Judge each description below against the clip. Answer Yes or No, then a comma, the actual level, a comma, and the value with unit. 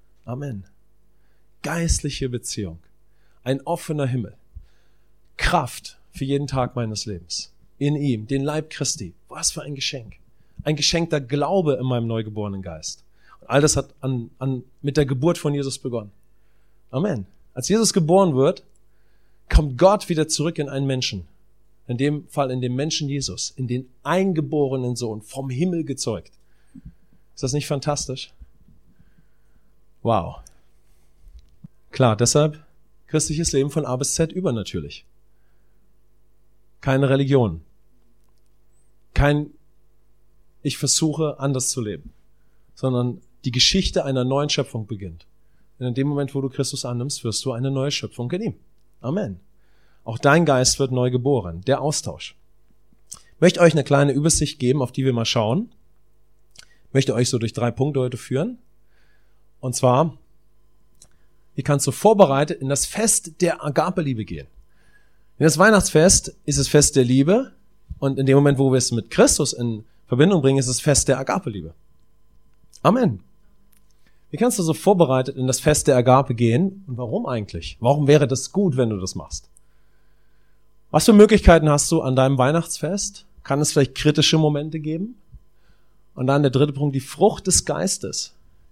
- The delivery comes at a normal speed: Yes, average, 150 wpm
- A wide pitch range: No, average, 5.0 semitones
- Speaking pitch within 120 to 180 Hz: Yes, low, 135 Hz